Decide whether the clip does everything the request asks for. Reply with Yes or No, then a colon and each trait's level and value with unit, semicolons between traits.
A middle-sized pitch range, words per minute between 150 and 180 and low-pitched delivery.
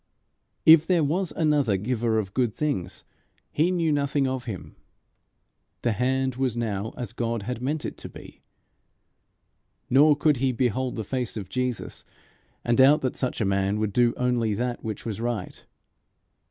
Yes: average, 3.7 semitones; average, 165 wpm; low, 125 Hz